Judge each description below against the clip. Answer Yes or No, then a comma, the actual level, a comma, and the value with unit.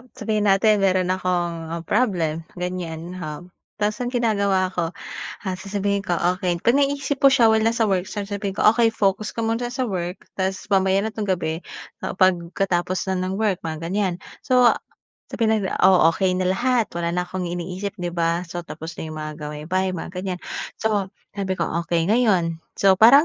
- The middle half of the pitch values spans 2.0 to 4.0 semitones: Yes, average, 3.4 semitones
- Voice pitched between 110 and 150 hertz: No, high, 190 Hz